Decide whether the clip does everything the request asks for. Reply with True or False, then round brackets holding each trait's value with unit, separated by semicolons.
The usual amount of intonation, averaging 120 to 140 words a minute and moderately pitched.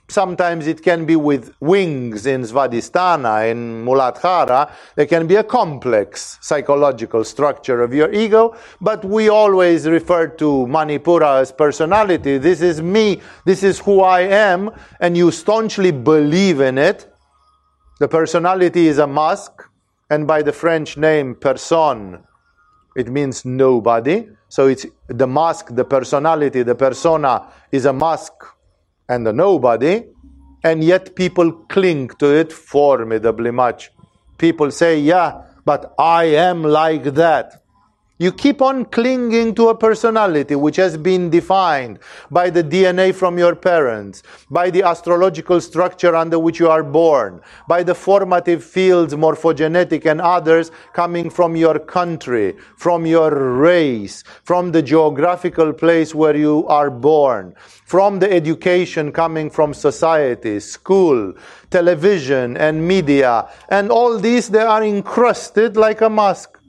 True (4.1 semitones; 135 wpm; 165 Hz)